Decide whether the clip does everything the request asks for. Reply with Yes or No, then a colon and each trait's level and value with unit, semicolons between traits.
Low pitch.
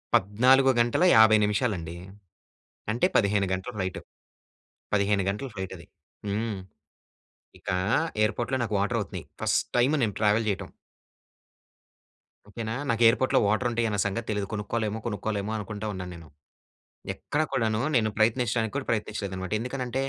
Yes: low, 110 Hz